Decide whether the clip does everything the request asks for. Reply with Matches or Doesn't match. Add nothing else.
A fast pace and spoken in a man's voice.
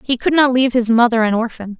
Doesn't match